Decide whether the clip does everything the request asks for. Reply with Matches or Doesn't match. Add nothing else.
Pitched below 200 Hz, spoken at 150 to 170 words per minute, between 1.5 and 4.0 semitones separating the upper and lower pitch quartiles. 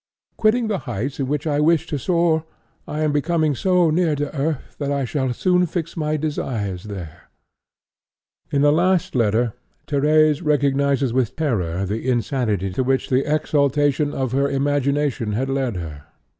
Matches